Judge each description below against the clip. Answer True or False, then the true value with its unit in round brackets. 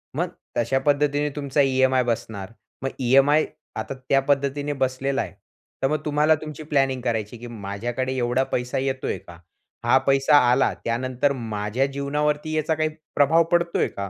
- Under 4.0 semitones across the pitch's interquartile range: True (3.1 semitones)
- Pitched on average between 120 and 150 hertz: True (135 Hz)